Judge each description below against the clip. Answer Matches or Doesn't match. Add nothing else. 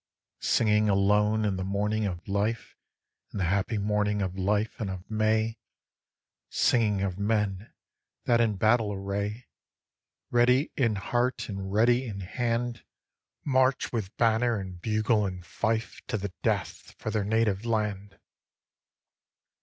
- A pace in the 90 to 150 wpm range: Matches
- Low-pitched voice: Matches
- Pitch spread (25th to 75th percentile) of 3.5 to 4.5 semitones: Doesn't match